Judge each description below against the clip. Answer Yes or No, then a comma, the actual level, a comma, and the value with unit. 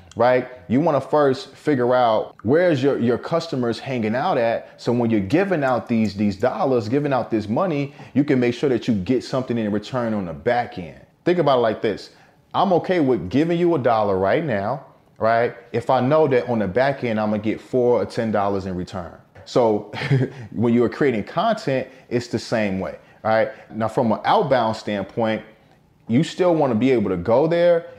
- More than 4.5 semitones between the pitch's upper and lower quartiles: No, average, 3.7 semitones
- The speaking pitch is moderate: No, low, 120 Hz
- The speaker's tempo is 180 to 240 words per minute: Yes, fast, 205 wpm